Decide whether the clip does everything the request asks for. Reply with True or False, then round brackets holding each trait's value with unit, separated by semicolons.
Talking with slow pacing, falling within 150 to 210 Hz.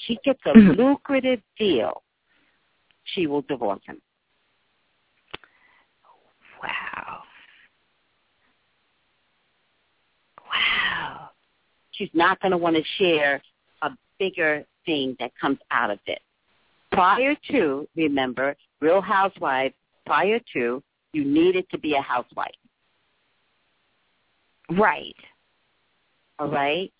True (95 wpm; 190 Hz)